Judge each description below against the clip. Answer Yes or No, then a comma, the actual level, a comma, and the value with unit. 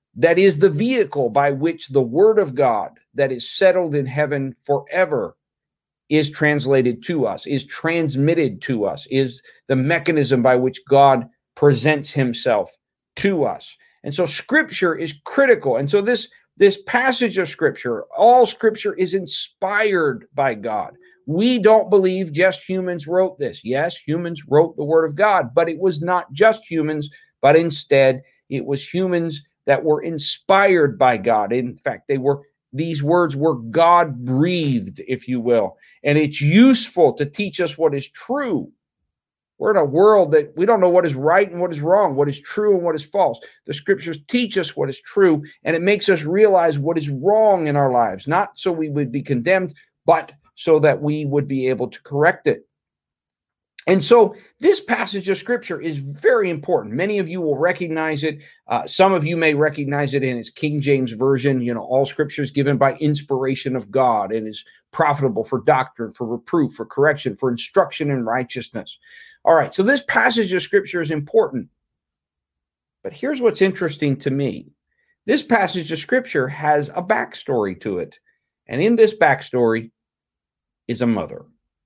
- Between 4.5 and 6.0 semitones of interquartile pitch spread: Yes, wide, 5.4 semitones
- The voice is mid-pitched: Yes, medium, 155 Hz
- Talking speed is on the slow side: No, average, 175 wpm